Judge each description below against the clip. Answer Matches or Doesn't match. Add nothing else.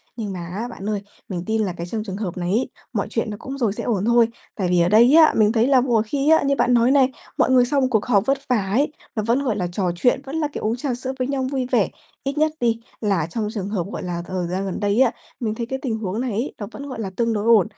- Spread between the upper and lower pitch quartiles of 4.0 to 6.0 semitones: Matches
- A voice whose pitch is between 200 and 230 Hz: Matches